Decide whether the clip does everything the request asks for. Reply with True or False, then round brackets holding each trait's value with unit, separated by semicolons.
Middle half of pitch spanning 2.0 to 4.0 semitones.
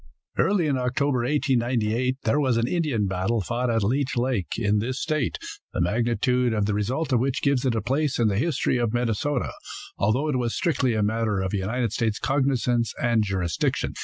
True (3.4 semitones)